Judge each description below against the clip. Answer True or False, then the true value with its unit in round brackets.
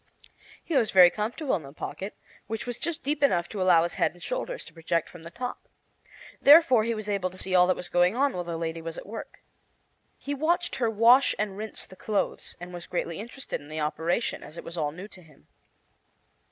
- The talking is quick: True (225 wpm)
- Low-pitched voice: False (190 Hz)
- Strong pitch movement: True (6.0 semitones)